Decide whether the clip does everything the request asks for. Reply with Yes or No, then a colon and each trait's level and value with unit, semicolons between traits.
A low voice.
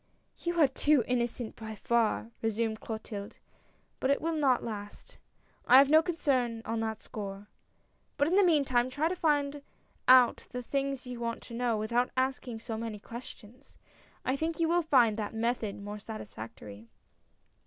No: high, 240 Hz